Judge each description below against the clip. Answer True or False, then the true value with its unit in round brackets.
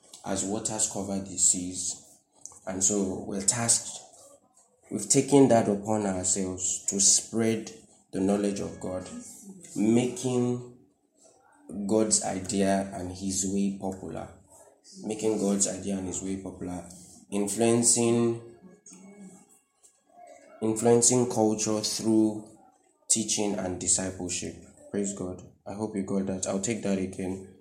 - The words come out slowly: True (115 wpm)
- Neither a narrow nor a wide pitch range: True (3.6 semitones)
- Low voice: True (100 Hz)